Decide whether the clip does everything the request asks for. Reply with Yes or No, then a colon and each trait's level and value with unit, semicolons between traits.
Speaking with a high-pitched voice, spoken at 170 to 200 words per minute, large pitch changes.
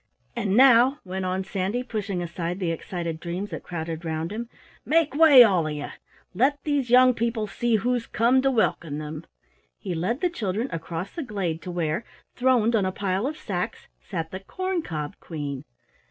Yes: high, 195 Hz; average, 185 wpm; wide, 6.4 semitones